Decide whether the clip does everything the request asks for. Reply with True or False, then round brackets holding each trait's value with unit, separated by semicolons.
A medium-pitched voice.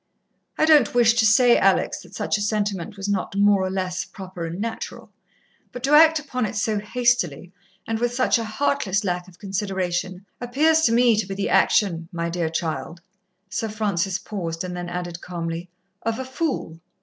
False (200 Hz)